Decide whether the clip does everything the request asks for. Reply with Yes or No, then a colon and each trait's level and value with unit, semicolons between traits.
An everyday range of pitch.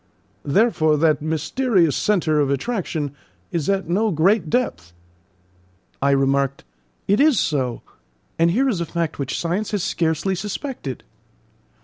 No: wide, 5.9 semitones